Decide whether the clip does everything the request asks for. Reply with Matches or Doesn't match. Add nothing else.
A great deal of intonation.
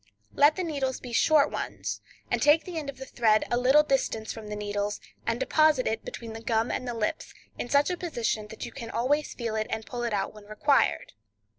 Doesn't match